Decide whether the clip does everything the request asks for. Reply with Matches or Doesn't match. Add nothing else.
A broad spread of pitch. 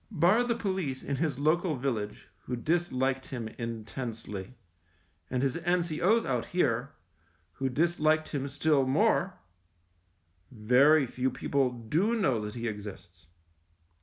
Matches